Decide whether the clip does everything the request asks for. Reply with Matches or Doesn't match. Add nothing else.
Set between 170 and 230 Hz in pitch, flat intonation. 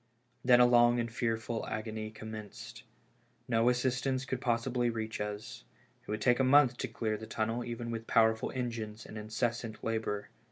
Doesn't match